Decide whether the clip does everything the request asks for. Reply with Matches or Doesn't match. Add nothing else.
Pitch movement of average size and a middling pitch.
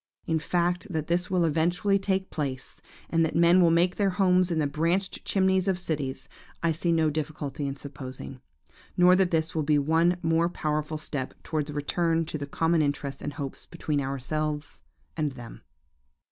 Matches